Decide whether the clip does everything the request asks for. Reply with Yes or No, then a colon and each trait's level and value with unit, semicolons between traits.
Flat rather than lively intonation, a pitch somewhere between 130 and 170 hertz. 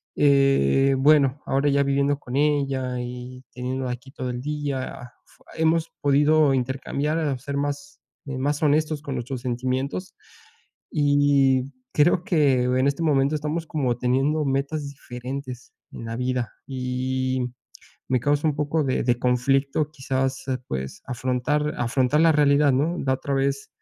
Yes: narrow, 2.3 semitones; low, 135 Hz